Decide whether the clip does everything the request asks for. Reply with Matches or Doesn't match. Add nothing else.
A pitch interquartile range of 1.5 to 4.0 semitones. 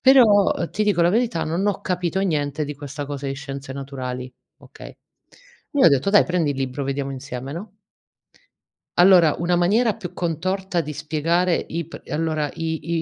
Doesn't match